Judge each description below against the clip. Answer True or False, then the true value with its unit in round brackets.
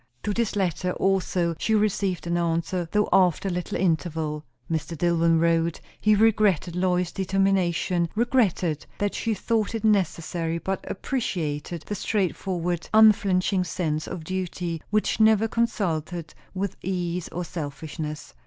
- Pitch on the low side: False (180 Hz)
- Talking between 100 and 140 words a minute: True (135 wpm)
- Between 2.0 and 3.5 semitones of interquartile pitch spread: True (3.1 semitones)